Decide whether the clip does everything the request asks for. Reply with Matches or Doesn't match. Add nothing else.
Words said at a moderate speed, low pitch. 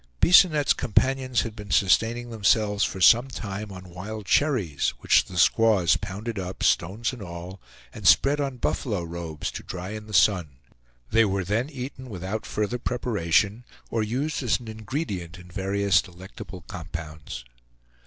Matches